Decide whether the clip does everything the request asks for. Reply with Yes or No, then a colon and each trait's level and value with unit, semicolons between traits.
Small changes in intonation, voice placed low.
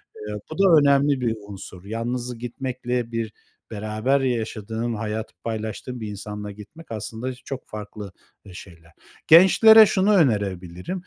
No: average, 4.1 semitones; low, 115 Hz